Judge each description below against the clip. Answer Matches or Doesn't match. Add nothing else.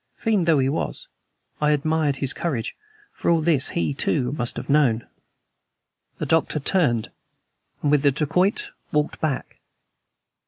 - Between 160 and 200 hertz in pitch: Doesn't match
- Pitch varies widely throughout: Doesn't match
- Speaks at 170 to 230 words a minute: Doesn't match